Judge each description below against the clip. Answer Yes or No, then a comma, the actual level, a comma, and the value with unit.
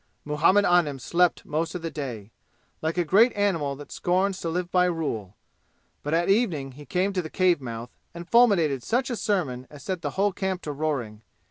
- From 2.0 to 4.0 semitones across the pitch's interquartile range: No, average, 4.6 semitones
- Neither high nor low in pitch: Yes, medium, 165 Hz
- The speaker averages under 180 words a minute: No, average, 200 wpm